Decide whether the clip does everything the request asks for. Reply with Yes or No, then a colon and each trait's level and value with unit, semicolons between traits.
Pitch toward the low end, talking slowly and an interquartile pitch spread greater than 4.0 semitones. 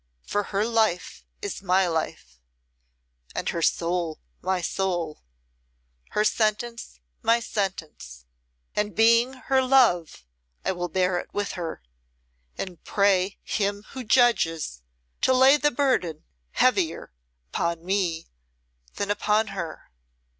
No: high, 195 Hz; slow, 120 wpm; average, 5.0 semitones